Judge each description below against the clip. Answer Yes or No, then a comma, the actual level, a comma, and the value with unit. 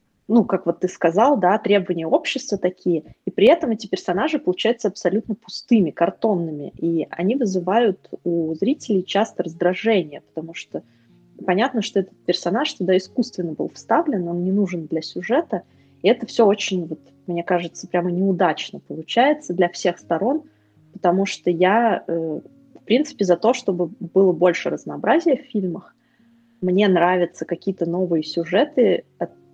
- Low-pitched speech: No, medium, 185 Hz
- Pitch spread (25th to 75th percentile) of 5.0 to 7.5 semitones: No, average, 4.1 semitones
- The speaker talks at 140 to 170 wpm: Yes, average, 145 wpm